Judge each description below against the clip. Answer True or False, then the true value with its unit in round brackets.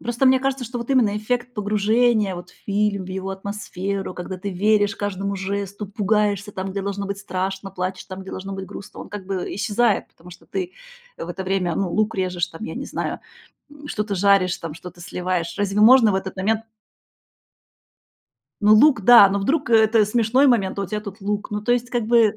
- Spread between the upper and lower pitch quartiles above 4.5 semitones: False (2.4 semitones)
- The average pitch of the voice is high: True (200 Hz)